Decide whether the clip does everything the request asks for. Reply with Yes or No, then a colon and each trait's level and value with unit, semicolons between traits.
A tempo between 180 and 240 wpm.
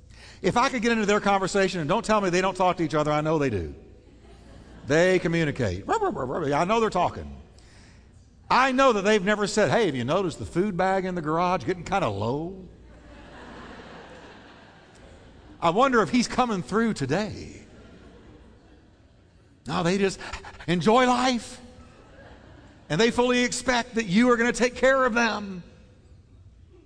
No: average, 160 wpm